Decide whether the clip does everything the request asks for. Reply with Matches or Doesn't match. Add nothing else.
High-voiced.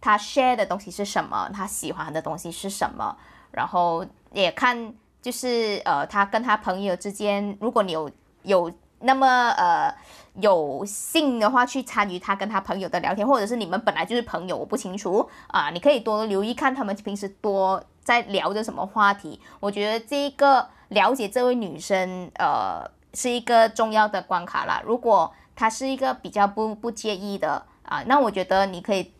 Matches